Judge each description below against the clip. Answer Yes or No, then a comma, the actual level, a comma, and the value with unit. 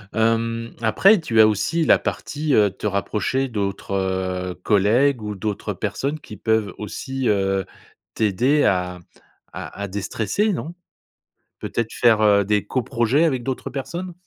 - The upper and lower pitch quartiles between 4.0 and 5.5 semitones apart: Yes, average, 4.8 semitones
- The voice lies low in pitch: Yes, low, 110 Hz